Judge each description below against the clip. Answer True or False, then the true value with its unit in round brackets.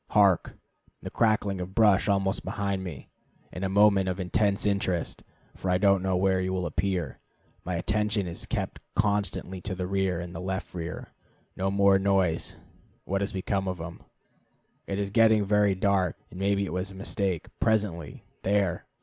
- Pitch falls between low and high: False (95 Hz)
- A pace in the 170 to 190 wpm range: True (175 wpm)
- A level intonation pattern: True (1.6 semitones)